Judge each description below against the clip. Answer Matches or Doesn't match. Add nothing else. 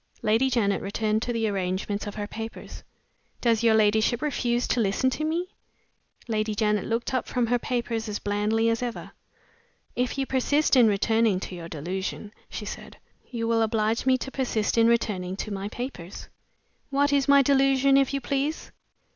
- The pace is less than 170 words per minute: Doesn't match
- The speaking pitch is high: Matches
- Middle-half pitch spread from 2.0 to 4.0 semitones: Matches